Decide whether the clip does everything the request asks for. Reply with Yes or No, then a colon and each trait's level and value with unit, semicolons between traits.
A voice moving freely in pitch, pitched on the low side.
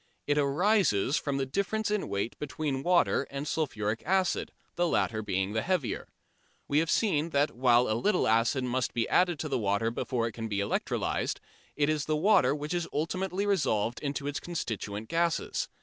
No: wide, 6.9 semitones; medium, 145 Hz